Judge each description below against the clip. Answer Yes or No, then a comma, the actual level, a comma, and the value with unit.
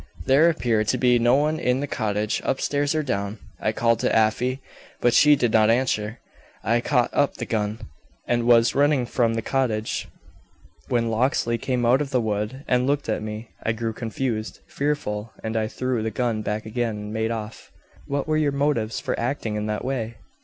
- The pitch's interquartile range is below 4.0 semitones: Yes, average, 3.3 semitones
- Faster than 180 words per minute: Yes, average, 195 wpm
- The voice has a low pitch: Yes, low, 120 Hz